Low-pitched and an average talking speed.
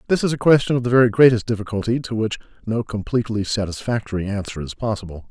Yes: low, 110 Hz; average, 190 wpm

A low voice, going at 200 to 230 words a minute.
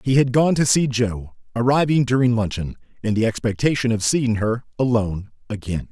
No: low, 115 Hz; average, 175 wpm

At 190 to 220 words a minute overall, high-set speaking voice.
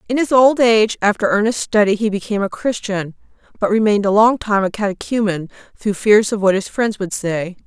Yes: fast, 205 wpm; high, 210 Hz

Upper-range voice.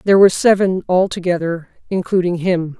No: medium, 180 Hz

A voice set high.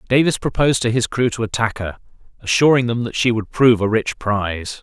No: low, 115 Hz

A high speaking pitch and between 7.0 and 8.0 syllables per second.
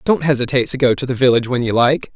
No: low, 130 Hz; 7.3 syllables/s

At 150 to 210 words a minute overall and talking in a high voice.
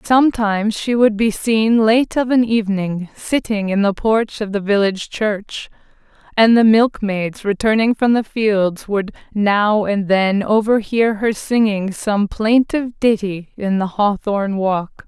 Yes: average, 155 wpm; high, 210 Hz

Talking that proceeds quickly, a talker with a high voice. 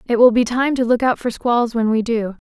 Yes: fast, 290 wpm; high, 235 Hz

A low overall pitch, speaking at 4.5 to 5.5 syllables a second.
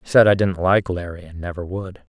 No: very low, 90 Hz; 6.1 syllables/s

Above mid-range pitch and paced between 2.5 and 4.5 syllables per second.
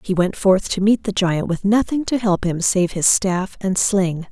Yes: high, 195 Hz; 4.3 syllables/s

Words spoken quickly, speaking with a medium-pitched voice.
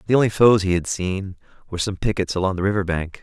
No: fast, 240 wpm; very low, 95 Hz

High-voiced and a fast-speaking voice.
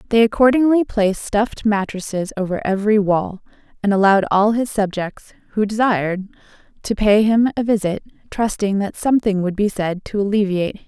No: high, 205 Hz; average, 165 wpm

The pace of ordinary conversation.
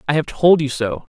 No: fast, 265 wpm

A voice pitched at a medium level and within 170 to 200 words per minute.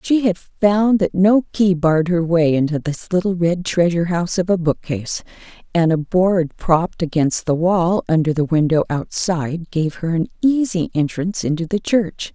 Yes: medium, 175 Hz; average, 180 wpm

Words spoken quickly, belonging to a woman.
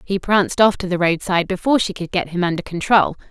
Yes: fast, 235 wpm; female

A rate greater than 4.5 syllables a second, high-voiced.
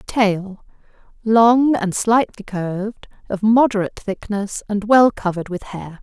No: 4.1 syllables/s; high, 210 Hz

